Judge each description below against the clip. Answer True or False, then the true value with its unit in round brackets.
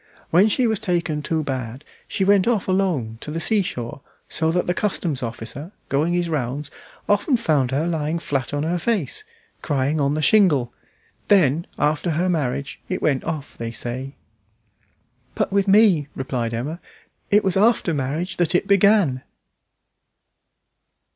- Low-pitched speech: False (160 Hz)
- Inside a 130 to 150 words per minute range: False (160 wpm)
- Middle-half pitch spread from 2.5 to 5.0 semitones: False (5.5 semitones)